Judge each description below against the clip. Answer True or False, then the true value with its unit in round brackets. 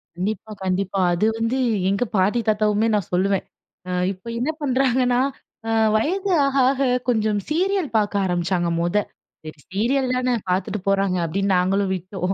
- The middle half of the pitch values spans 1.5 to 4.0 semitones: False (4.9 semitones)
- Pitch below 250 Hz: True (210 Hz)